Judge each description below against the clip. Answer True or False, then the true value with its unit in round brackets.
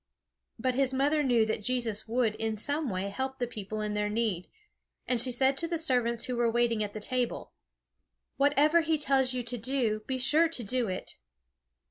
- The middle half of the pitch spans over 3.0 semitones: True (3.5 semitones)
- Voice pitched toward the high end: True (245 Hz)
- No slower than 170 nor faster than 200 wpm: True (195 wpm)